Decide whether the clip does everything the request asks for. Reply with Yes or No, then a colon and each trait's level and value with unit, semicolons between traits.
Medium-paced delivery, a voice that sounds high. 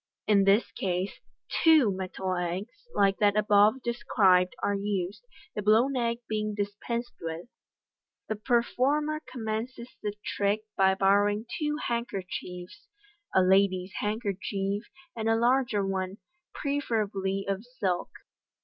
No: slow, 120 wpm; high, 205 Hz